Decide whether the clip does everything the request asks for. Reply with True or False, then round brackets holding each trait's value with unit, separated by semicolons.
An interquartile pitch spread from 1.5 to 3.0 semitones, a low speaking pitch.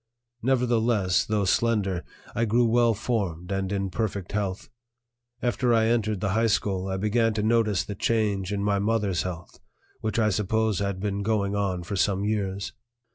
True (2.6 semitones; 105 Hz)